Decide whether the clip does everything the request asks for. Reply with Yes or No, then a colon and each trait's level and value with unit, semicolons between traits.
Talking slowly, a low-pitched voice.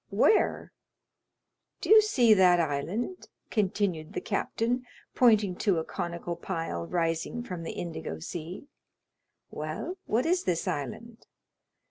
No: slow, 120 wpm; medium, 185 Hz